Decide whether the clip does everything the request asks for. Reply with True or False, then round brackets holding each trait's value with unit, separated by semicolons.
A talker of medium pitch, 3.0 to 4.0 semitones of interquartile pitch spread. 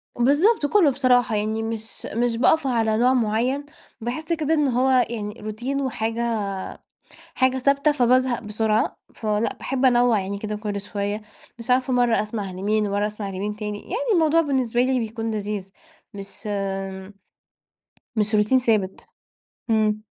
False (230 Hz; 3.6 semitones)